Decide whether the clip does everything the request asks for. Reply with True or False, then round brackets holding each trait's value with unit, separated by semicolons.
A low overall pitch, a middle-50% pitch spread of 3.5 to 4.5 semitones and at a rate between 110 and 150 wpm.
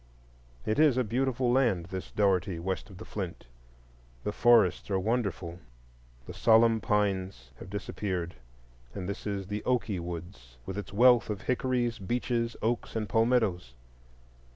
True (105 Hz; 4.2 semitones; 145 wpm)